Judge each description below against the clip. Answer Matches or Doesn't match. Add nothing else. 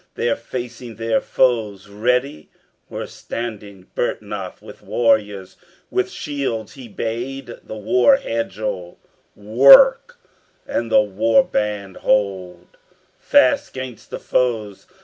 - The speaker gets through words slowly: Matches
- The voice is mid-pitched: Doesn't match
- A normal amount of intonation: Matches